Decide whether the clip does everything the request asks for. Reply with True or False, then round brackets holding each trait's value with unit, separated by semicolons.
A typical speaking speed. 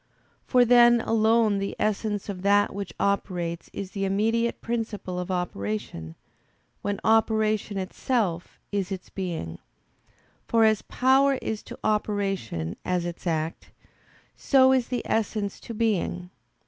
False (130 wpm)